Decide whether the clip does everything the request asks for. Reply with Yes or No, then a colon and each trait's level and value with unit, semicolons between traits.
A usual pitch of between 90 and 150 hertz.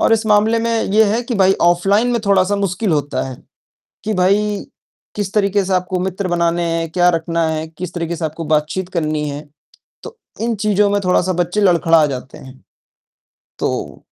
No: medium, 185 Hz